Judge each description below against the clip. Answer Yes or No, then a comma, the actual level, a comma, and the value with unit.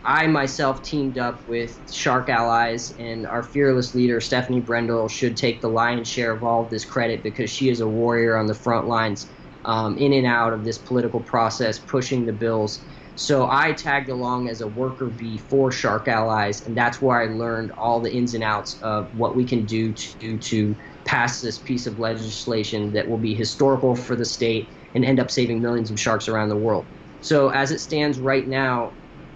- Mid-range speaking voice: No, low, 120 Hz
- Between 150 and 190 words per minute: No, fast, 205 wpm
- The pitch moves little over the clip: Yes, narrow, 2.3 semitones